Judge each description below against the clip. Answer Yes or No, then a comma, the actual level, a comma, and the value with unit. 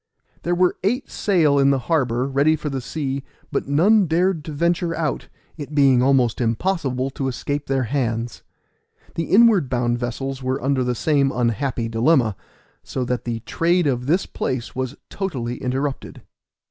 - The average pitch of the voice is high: No, low, 135 Hz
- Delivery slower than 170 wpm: Yes, average, 160 wpm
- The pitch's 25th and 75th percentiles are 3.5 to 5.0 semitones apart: Yes, average, 4.4 semitones